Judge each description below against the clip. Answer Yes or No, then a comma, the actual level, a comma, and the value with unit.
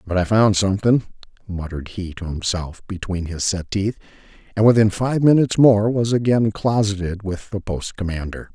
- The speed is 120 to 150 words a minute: No, average, 170 wpm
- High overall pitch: No, low, 100 Hz